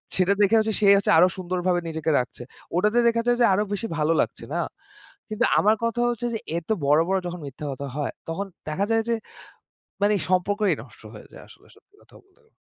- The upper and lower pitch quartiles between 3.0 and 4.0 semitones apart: No, average, 4.5 semitones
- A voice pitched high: Yes, high, 200 Hz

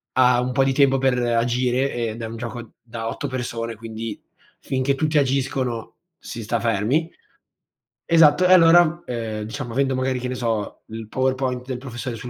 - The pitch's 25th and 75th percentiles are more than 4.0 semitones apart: No, average, 2.7 semitones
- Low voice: Yes, low, 125 Hz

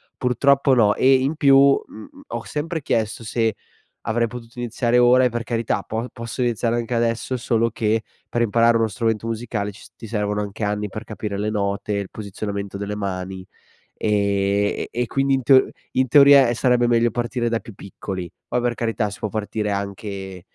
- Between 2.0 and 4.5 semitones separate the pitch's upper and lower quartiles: Yes, average, 2.9 semitones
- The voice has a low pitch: Yes, low, 115 Hz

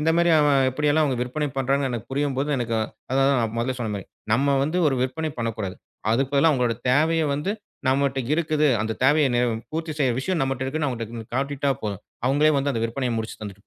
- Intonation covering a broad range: No, average, 4.0 semitones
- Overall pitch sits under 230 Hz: Yes, low, 135 Hz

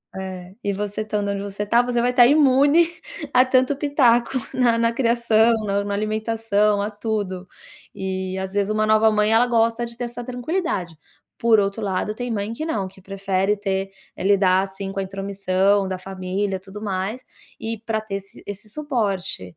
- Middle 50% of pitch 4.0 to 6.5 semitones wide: No, average, 3.3 semitones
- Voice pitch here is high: Yes, high, 210 Hz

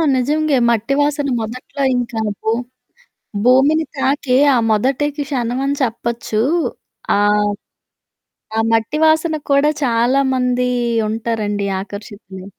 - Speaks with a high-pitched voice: Yes, very high, 250 Hz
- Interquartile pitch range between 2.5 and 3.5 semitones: No, average, 4.0 semitones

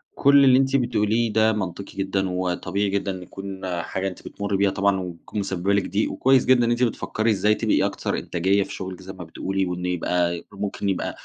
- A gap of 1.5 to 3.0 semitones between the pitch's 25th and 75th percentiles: Yes, narrow, 2.5 semitones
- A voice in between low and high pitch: No, low, 100 Hz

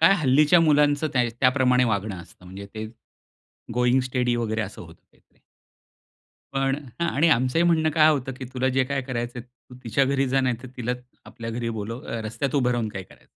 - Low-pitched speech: Yes, low, 125 Hz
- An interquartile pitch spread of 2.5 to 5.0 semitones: Yes, average, 2.9 semitones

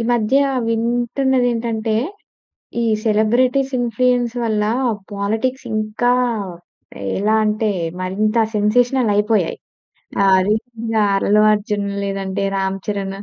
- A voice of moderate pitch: No, high, 220 Hz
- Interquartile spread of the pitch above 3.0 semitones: No, average, 2.7 semitones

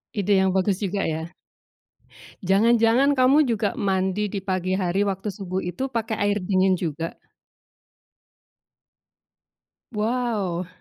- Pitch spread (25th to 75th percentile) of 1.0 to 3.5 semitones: Yes, average, 2.9 semitones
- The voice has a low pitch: No, high, 195 Hz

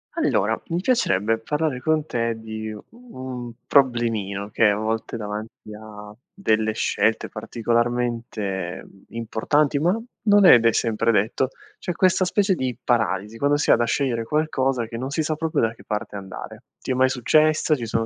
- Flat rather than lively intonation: No, average, 5.0 semitones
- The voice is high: No, low, 120 Hz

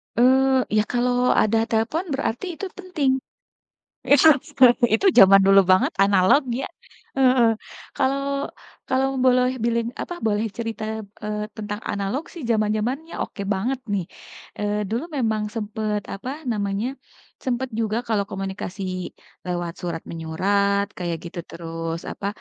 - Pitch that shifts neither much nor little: Yes, average, 4.4 semitones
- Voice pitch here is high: Yes, high, 215 Hz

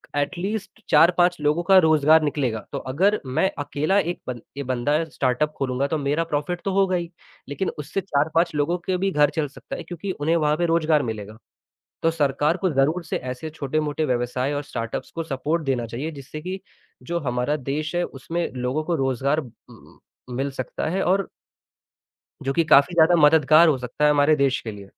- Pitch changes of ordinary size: Yes, average, 3.7 semitones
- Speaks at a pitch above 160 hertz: No, medium, 150 Hz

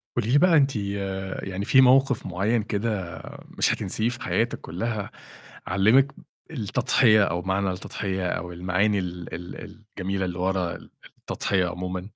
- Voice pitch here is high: No, low, 100 Hz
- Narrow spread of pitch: No, average, 3.8 semitones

